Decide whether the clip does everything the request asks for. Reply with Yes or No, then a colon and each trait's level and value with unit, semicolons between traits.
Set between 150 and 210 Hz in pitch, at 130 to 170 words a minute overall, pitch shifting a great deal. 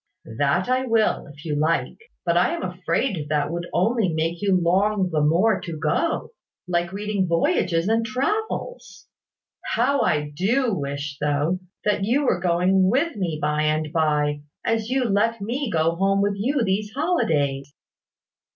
Yes: medium, 185 Hz; average, 160 wpm; wide, 6.2 semitones